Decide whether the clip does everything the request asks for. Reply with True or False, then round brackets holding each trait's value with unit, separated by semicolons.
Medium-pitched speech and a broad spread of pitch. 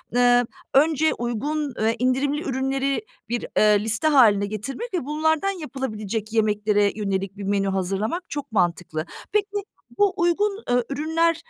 False (250 Hz; 6.7 semitones)